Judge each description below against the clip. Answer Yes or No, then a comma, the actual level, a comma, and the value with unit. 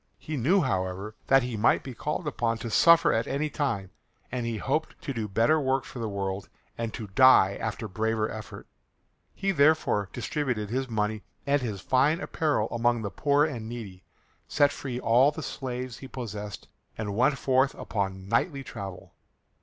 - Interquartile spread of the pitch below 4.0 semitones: No, average, 4.6 semitones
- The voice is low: Yes, low, 120 Hz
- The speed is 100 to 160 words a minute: No, average, 175 wpm